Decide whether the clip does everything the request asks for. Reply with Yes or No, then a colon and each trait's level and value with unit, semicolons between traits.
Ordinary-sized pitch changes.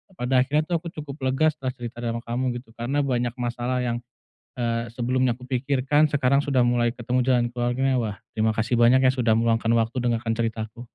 No: narrow, 1.9 semitones